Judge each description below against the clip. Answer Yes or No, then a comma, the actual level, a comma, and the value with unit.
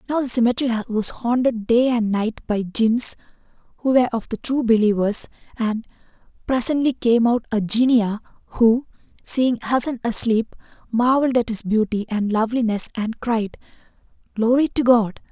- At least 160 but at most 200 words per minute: No, average, 145 wpm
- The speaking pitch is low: No, high, 230 Hz